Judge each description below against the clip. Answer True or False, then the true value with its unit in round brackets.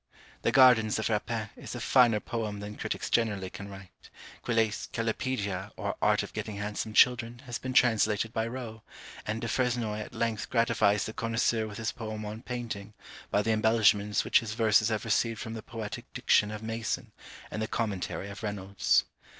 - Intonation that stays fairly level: True (1.8 semitones)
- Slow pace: False (180 wpm)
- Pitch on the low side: True (110 Hz)